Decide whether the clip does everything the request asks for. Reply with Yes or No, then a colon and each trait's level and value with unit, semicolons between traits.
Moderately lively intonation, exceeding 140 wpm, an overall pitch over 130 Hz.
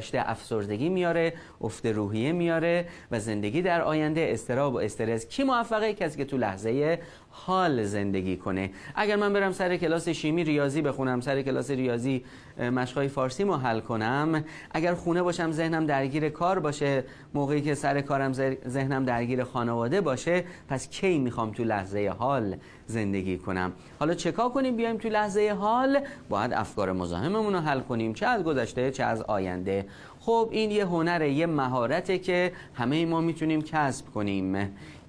No: wide, 6.6 semitones; fast, 155 wpm; medium, 140 Hz